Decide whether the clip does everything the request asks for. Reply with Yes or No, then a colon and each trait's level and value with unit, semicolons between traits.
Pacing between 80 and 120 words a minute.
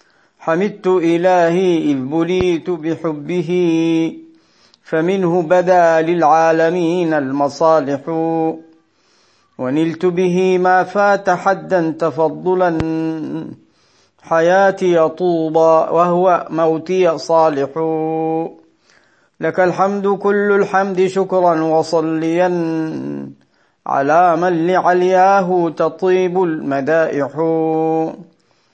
No: slow, 65 wpm